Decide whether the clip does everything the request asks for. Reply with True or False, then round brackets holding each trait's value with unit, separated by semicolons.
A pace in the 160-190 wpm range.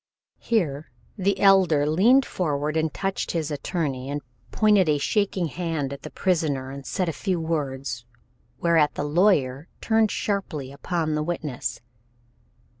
False (140 wpm)